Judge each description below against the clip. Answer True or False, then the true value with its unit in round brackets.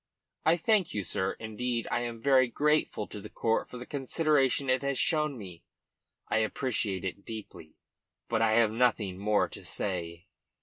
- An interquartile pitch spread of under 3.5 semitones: False (4.7 semitones)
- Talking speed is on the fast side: False (170 wpm)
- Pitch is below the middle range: True (115 Hz)